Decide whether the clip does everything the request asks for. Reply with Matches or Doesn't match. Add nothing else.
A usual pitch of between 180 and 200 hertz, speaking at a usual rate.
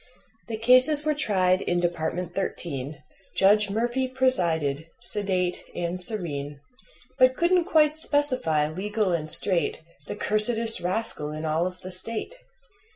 Doesn't match